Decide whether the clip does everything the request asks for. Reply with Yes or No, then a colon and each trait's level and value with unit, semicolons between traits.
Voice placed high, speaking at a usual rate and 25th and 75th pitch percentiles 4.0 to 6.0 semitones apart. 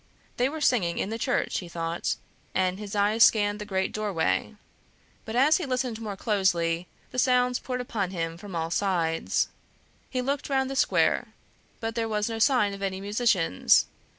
Yes: high, 210 Hz; average, 180 wpm; average, 4.8 semitones